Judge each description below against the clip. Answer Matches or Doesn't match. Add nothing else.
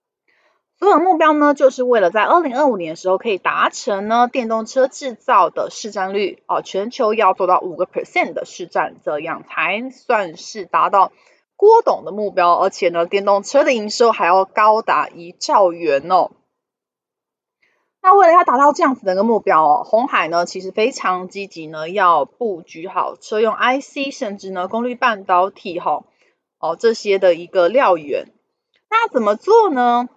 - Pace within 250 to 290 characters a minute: Matches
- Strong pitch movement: Matches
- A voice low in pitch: Doesn't match